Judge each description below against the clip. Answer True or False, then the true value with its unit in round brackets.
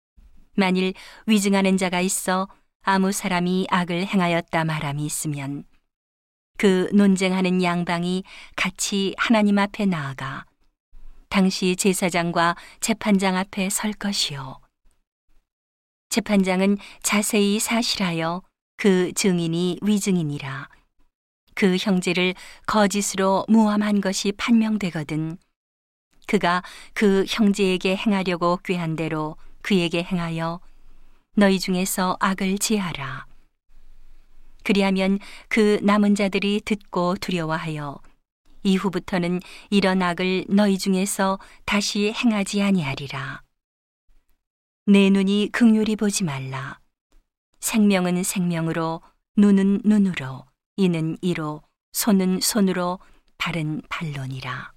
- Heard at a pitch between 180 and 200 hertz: True (185 Hz)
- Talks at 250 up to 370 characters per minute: False (225 characters per minute)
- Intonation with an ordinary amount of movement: True (3.2 semitones)